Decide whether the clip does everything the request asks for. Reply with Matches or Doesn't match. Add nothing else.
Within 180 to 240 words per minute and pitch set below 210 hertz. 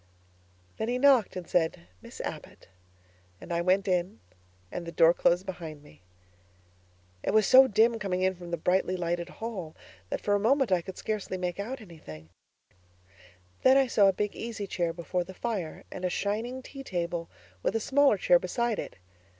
Matches